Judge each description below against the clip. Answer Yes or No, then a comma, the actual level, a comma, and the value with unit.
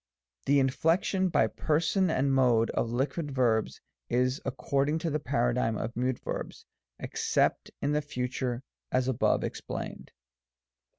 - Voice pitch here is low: Yes, low, 130 Hz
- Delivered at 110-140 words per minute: Yes, slow, 135 wpm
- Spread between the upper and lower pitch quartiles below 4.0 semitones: Yes, average, 3.2 semitones